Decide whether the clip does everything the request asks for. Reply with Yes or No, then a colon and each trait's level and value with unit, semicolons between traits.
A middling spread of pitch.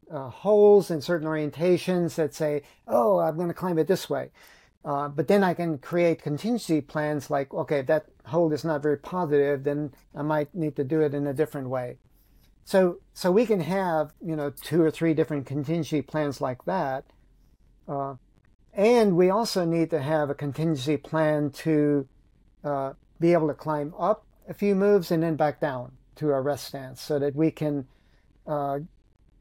Yes: average, 3.0 semitones